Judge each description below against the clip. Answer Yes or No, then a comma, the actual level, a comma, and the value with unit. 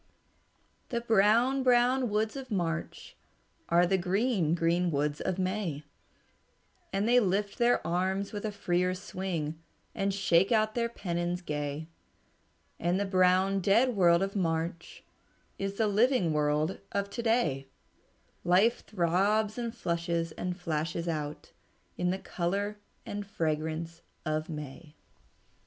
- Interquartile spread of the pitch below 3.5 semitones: No, average, 3.9 semitones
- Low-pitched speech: No, medium, 185 Hz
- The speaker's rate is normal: No, slow, 130 wpm